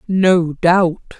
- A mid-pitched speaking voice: Yes, medium, 175 Hz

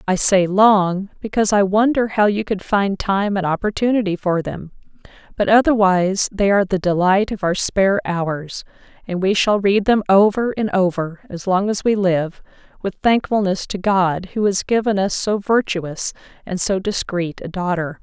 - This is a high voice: Yes, high, 195 Hz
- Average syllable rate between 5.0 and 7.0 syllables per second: No, 4.7 syllables/s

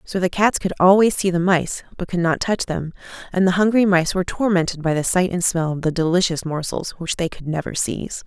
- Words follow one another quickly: Yes, fast, 240 wpm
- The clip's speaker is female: Yes, female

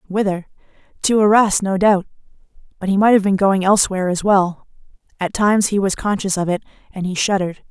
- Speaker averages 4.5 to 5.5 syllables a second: No, 6.1 syllables/s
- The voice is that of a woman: Yes, female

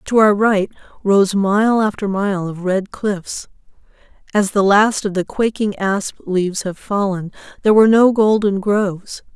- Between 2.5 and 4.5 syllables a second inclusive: Yes, 4.4 syllables/s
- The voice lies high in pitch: Yes, high, 200 Hz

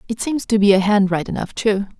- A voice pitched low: No, high, 205 Hz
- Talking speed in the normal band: No, fast, 270 wpm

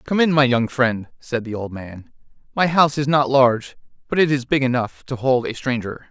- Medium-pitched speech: No, low, 130 Hz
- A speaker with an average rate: No, fast, 225 wpm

